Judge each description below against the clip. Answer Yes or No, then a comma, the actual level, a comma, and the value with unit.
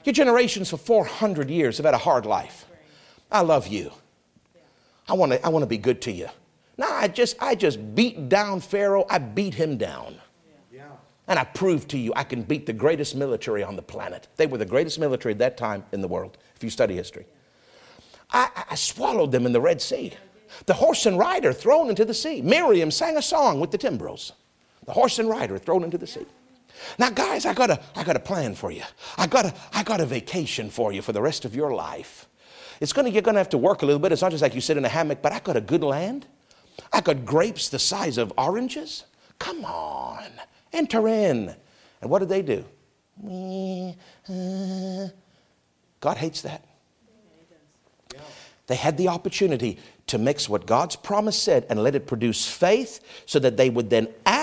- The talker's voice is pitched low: No, high, 190 Hz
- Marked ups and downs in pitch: Yes, wide, 7.6 semitones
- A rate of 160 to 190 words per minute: No, fast, 205 wpm